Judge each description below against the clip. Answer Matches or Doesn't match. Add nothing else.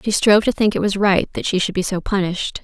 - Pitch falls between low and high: Doesn't match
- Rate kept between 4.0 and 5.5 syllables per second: Doesn't match